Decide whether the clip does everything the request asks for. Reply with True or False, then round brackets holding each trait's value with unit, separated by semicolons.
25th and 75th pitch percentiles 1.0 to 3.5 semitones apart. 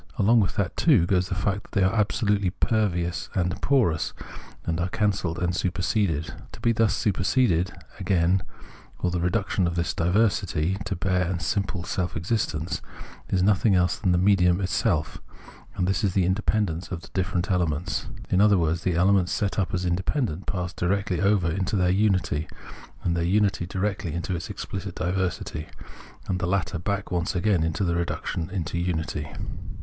True (2.5 semitones)